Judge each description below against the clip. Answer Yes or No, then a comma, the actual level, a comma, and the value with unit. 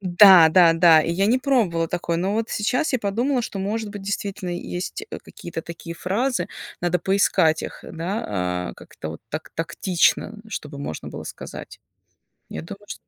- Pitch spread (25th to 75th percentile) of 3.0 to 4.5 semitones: Yes, average, 3.9 semitones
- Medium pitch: Yes, medium, 180 Hz